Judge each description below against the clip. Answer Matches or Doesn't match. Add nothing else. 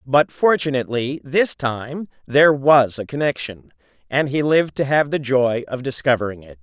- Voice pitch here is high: Doesn't match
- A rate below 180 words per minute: Matches